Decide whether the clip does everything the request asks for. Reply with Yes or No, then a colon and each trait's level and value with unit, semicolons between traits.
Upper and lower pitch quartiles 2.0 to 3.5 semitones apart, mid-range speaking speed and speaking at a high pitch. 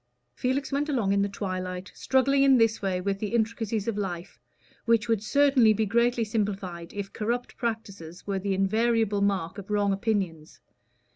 Yes: average, 3.1 semitones; average, 165 wpm; high, 210 Hz